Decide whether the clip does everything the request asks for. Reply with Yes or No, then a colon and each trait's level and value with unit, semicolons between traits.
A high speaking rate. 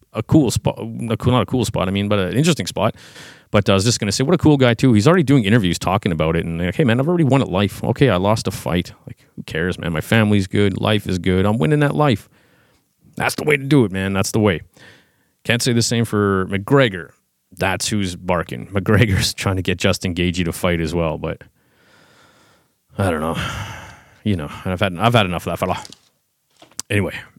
Yes: fast, 230 wpm